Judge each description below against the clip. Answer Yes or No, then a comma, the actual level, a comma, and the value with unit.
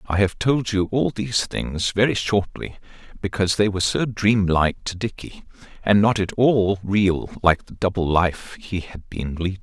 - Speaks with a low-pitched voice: Yes, low, 100 Hz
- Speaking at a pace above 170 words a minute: Yes, average, 185 wpm